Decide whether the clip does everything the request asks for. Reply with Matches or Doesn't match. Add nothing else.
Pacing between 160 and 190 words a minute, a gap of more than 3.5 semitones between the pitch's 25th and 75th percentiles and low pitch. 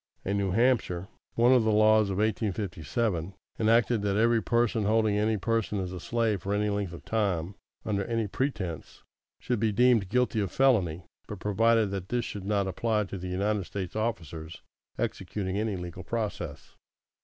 Doesn't match